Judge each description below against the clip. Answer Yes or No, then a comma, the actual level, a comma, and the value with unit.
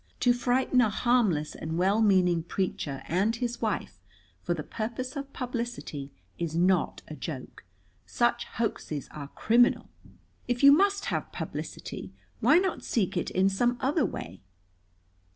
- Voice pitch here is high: Yes, high, 220 Hz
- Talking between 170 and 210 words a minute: No, average, 145 wpm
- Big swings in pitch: Yes, wide, 6.3 semitones